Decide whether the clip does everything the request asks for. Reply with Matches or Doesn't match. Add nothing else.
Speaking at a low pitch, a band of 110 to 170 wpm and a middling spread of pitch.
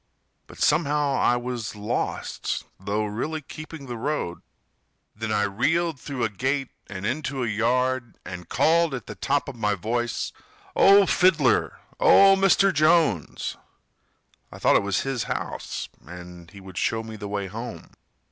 Doesn't match